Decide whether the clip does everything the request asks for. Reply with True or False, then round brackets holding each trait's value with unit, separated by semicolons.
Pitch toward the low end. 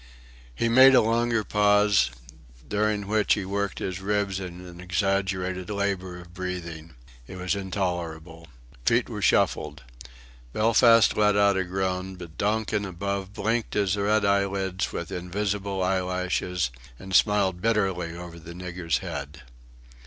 True (95 Hz)